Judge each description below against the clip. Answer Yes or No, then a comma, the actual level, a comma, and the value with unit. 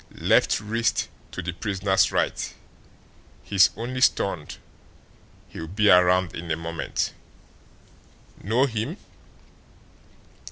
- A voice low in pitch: Yes, very low, 95 Hz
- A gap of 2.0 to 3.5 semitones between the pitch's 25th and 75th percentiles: No, average, 4.3 semitones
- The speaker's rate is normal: No, slow, 95 wpm